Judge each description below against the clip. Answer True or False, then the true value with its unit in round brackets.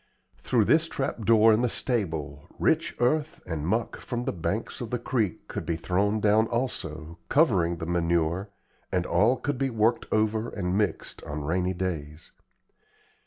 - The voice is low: True (100 Hz)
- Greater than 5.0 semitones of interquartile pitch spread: True (5.5 semitones)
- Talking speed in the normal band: True (165 wpm)